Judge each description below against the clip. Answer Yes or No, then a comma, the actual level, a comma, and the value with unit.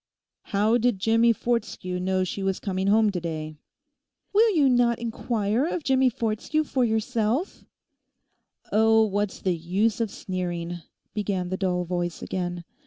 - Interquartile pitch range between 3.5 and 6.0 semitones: Yes, average, 4.3 semitones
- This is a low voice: No, high, 210 Hz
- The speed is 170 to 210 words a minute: No, average, 150 wpm